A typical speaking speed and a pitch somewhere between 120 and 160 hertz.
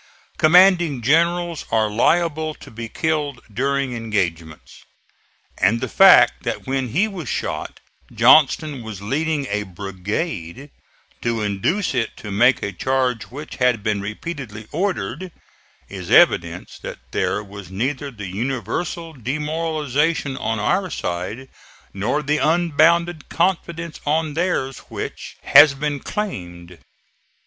No: slow, 120 wpm; low, 135 Hz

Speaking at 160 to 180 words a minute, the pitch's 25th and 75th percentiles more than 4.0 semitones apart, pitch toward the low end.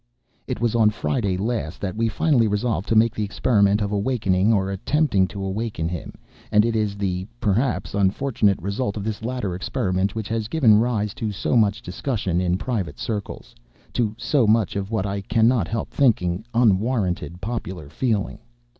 No: average, 170 wpm; average, 3.0 semitones; low, 105 Hz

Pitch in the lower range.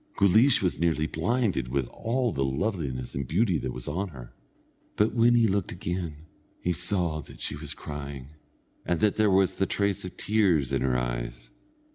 Yes: very low, 85 Hz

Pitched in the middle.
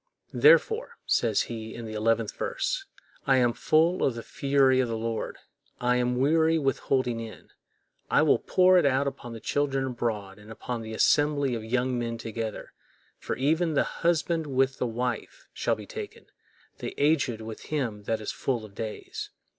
No: low, 125 Hz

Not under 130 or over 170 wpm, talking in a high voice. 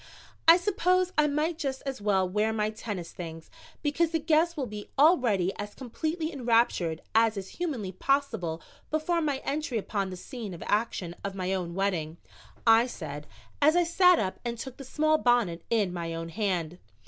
No: average, 180 wpm; high, 225 Hz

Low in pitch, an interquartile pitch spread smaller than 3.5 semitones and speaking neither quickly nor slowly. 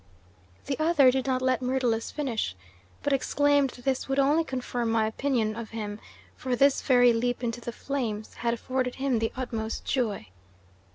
No: very high, 250 Hz; average, 2.9 semitones; average, 170 wpm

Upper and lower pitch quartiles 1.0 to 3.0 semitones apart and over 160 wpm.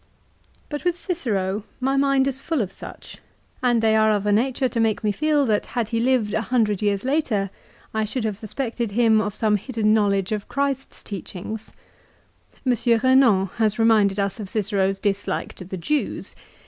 No: average, 4.0 semitones; average, 180 wpm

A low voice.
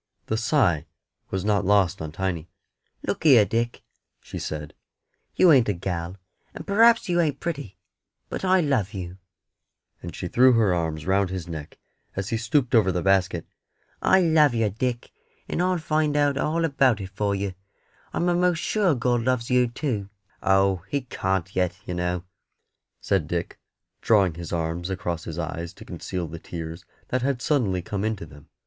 Yes: low, 100 Hz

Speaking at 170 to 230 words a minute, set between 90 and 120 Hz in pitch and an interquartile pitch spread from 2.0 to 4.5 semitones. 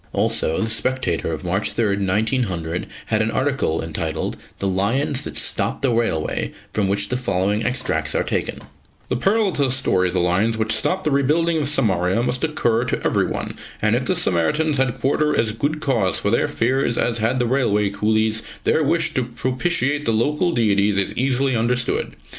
No: average, 185 wpm; low, 115 Hz; average, 5.2 semitones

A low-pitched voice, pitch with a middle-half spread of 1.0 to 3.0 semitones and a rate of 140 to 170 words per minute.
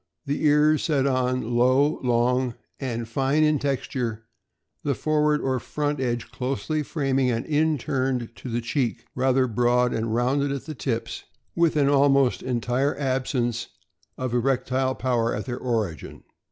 Yes: low, 130 Hz; average, 2.7 semitones; average, 150 wpm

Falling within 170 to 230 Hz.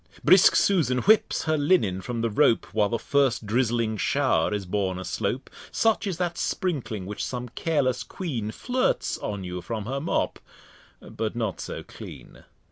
No: low, 120 Hz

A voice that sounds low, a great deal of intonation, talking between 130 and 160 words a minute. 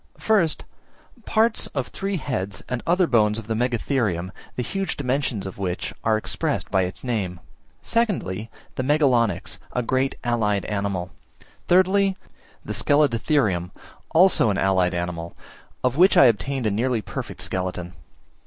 Yes: low, 115 Hz; wide, 6.8 semitones; average, 140 wpm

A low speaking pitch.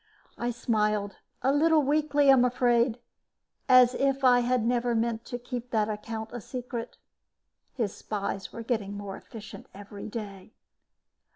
No: high, 235 Hz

